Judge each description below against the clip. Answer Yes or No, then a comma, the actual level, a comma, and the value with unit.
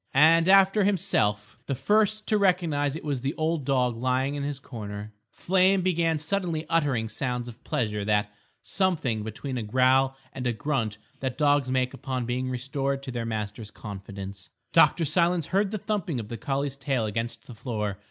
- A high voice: No, low, 135 Hz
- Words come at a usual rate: Yes, average, 175 wpm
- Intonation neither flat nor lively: No, wide, 6.0 semitones